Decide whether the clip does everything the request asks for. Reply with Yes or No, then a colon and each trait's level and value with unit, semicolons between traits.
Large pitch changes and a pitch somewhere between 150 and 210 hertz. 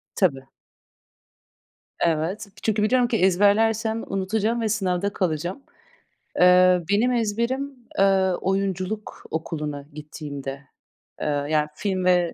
No: average, 4.1 semitones; high, 190 Hz